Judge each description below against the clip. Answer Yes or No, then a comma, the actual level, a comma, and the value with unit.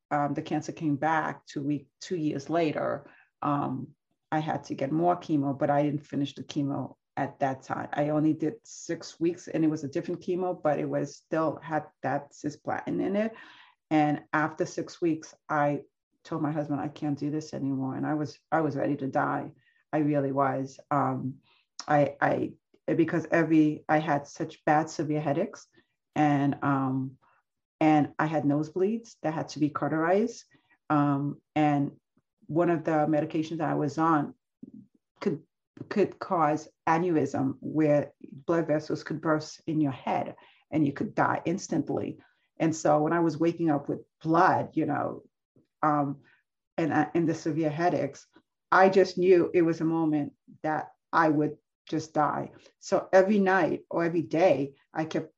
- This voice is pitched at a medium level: Yes, medium, 155 Hz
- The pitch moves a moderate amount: No, narrow, 2.2 semitones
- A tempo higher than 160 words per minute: Yes, average, 170 wpm